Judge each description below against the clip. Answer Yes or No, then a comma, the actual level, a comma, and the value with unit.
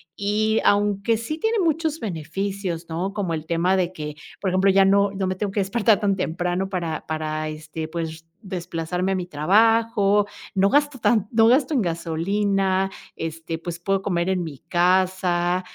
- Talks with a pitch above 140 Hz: Yes, high, 190 Hz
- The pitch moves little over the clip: No, average, 3.4 semitones